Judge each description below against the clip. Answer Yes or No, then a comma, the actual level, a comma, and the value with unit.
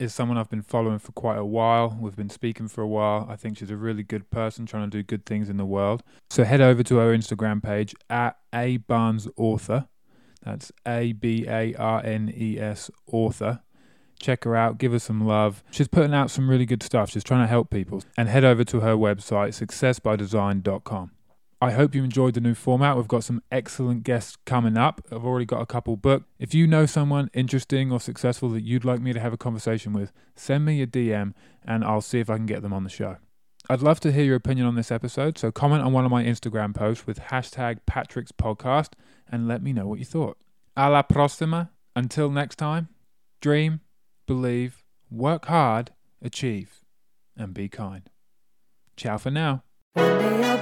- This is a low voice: Yes, low, 120 Hz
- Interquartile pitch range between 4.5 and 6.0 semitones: No, average, 3.1 semitones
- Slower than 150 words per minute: No, fast, 205 wpm